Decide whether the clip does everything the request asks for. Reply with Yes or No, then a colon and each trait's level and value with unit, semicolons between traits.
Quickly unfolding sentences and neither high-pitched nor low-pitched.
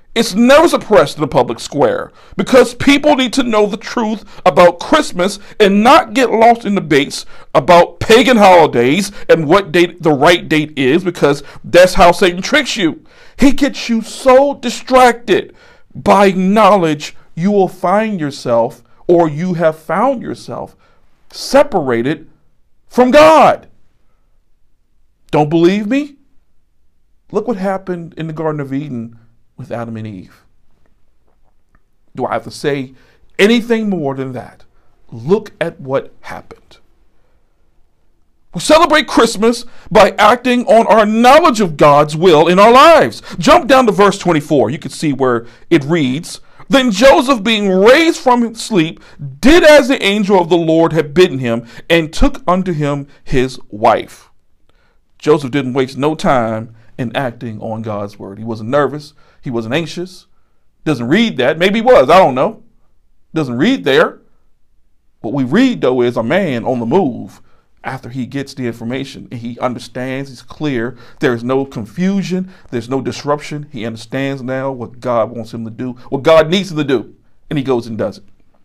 No: average, 160 wpm; medium, 175 Hz